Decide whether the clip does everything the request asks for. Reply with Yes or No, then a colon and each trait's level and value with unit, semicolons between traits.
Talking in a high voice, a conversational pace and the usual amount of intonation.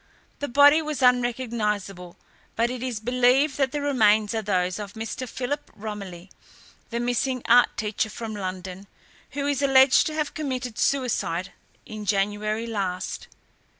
Yes: high, 230 Hz; average, 145 wpm; average, 4.1 semitones